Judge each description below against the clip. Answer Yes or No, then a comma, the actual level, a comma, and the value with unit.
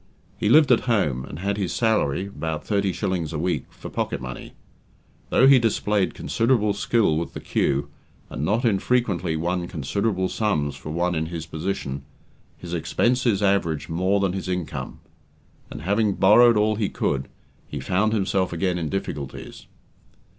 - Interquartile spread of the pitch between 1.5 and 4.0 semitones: No, average, 4.7 semitones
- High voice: No, very low, 95 Hz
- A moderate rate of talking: Yes, average, 160 wpm